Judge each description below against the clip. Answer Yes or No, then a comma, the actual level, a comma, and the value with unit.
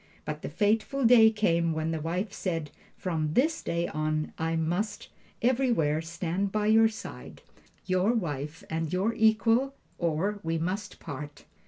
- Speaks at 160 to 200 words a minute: No, average, 150 wpm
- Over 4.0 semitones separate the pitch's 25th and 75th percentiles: Yes, average, 5.3 semitones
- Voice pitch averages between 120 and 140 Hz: No, medium, 180 Hz